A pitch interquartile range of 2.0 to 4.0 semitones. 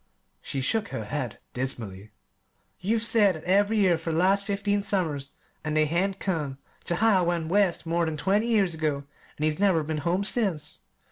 No: average, 4.8 semitones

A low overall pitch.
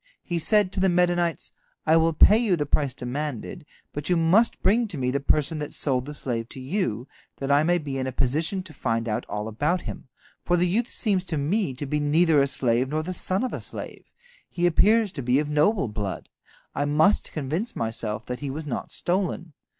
No: medium, 155 Hz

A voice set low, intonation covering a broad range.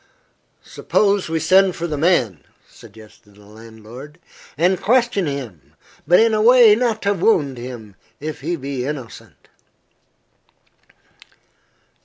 No: medium, 150 Hz; wide, 8.9 semitones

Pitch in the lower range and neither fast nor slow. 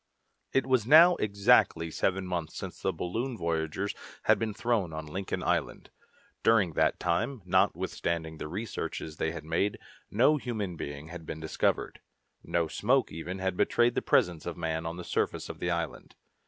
Yes: very low, 90 Hz; average, 170 wpm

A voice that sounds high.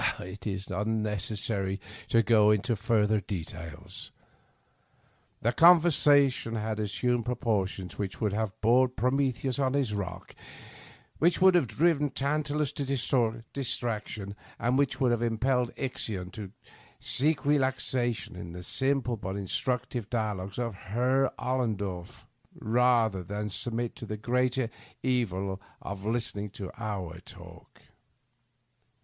No: low, 115 Hz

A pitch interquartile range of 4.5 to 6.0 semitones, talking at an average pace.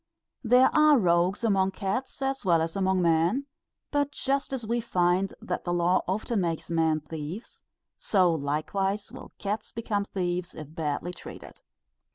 Yes: average, 4.8 semitones; average, 155 wpm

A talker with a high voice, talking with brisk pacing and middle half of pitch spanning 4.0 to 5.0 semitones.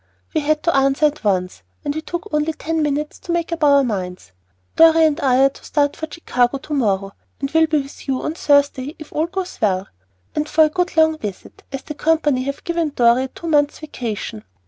No: very high, 295 Hz; fast, 220 wpm; average, 3.4 semitones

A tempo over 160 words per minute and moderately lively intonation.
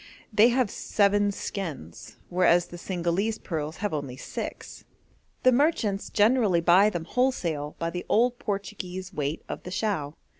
No: average, 145 wpm; average, 4.0 semitones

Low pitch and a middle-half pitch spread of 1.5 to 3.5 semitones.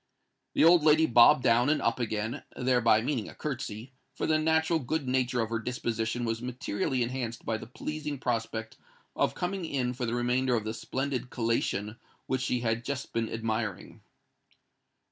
Yes: low, 125 Hz; average, 3.0 semitones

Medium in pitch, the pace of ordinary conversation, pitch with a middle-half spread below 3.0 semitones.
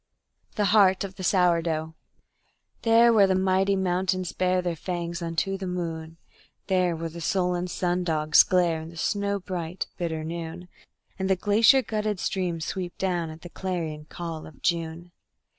Yes: medium, 180 Hz; average, 160 wpm; narrow, 2.4 semitones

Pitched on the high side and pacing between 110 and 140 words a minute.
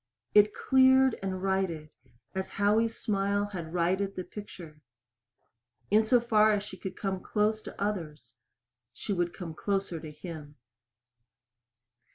Yes: high, 195 Hz; slow, 135 wpm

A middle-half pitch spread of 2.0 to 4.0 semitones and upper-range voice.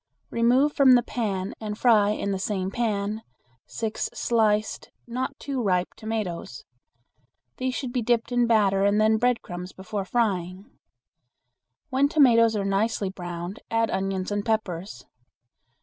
Yes: average, 3.4 semitones; high, 215 Hz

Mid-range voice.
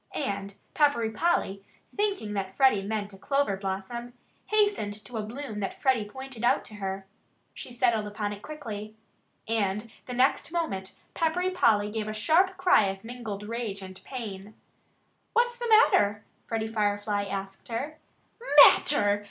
No: high, 220 Hz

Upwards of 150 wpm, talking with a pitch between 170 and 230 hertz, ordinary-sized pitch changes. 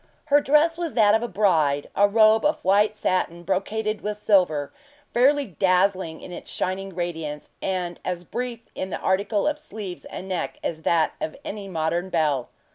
Yes: average, 175 wpm; high, 190 Hz; average, 3.9 semitones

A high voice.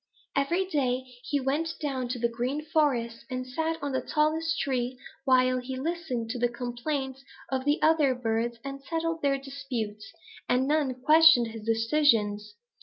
Yes: very high, 265 Hz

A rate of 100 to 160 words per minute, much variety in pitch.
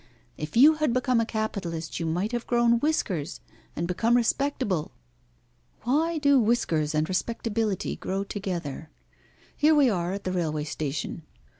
Yes: average, 145 wpm; wide, 6.3 semitones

